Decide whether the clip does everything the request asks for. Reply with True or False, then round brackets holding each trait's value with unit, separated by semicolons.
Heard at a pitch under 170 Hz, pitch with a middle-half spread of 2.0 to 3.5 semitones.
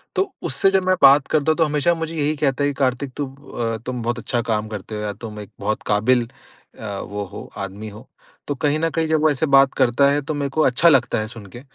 False (135 Hz; 5.3 semitones)